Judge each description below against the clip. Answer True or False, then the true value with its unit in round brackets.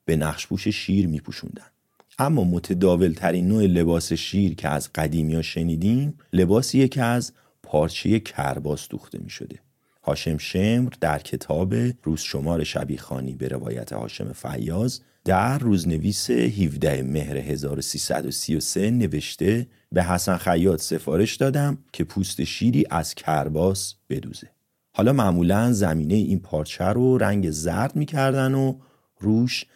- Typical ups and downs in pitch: False (6.7 semitones)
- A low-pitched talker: True (95 Hz)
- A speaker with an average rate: True (130 wpm)